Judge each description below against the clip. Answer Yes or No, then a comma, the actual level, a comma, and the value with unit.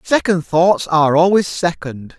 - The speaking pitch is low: No, medium, 155 Hz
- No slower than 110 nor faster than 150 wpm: Yes, slow, 135 wpm